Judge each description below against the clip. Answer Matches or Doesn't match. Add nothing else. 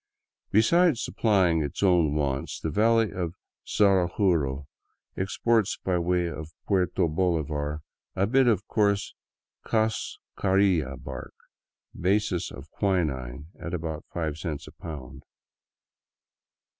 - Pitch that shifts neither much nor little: Matches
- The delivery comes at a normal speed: Doesn't match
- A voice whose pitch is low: Matches